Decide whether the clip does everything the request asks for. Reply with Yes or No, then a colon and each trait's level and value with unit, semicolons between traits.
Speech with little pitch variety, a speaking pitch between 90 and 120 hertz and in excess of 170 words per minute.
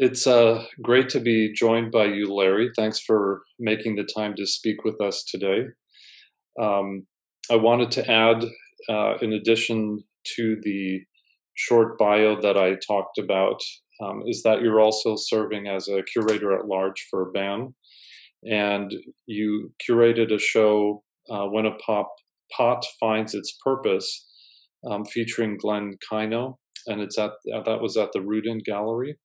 No: narrow, 1.9 semitones; low, 110 Hz; average, 150 wpm